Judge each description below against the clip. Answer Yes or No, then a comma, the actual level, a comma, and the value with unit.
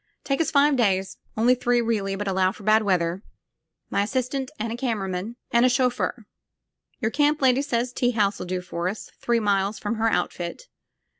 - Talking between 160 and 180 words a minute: No, average, 195 wpm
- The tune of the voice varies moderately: Yes, average, 4.3 semitones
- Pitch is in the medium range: No, high, 225 Hz